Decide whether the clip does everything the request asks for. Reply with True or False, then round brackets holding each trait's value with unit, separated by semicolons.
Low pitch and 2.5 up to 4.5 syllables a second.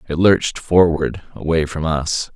True (80 Hz; 4.4 syllables/s)